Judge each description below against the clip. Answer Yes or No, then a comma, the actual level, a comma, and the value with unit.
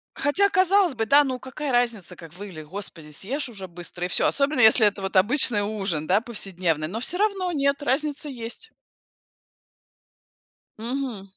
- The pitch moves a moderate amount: No, wide, 6.8 semitones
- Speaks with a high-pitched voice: Yes, high, 230 Hz